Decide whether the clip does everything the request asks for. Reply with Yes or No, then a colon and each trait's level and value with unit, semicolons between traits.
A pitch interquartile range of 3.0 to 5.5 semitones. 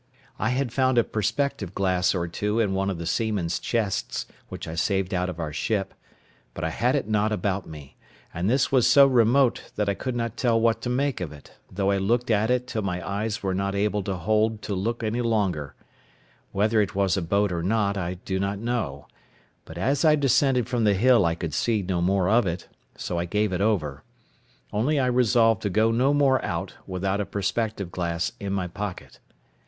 Yes: average, 3.9 semitones